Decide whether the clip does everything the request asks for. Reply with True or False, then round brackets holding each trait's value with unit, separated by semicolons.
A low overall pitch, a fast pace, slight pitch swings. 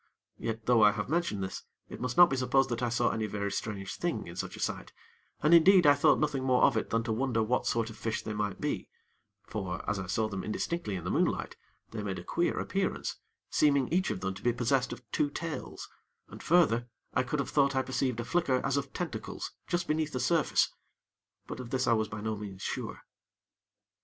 False (120 Hz; 225 wpm; 4.7 semitones)